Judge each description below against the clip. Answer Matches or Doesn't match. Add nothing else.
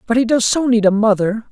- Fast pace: Matches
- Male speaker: Matches